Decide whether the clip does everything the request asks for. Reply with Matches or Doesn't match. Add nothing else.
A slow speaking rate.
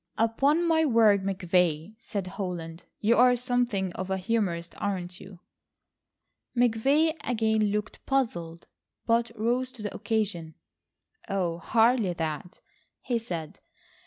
Matches